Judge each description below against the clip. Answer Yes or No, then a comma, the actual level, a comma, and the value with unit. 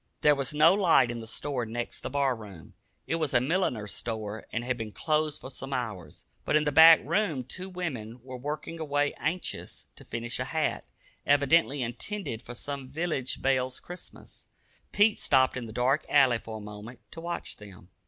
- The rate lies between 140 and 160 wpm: No, average, 190 wpm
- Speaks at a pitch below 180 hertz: Yes, low, 135 Hz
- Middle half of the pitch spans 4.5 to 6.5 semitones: Yes, average, 4.8 semitones